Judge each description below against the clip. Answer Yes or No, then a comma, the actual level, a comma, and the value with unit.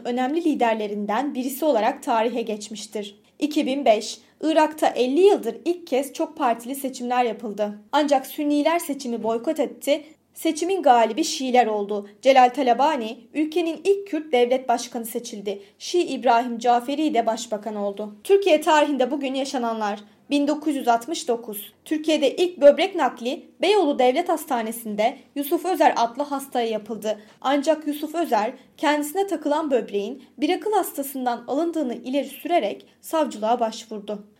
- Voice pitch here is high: Yes, very high, 260 Hz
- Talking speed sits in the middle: Yes, average, 120 wpm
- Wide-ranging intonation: No, average, 5.0 semitones